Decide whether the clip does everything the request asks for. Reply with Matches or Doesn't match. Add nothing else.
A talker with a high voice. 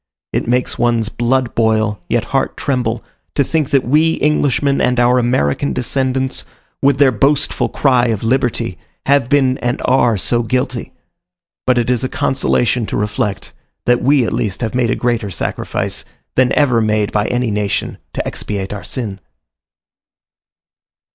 Doesn't match